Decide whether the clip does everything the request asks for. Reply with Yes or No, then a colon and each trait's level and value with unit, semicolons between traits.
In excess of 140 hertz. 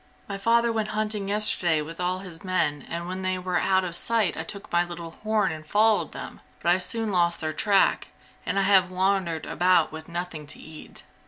Yes: medium, 185 Hz